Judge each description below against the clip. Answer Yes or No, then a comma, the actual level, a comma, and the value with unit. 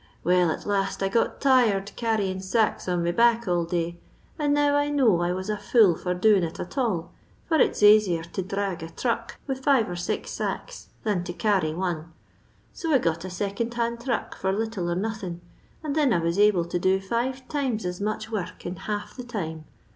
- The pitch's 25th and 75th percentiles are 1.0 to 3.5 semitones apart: No, average, 4.8 semitones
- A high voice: Yes, high, 200 Hz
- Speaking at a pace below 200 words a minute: No, fast, 205 wpm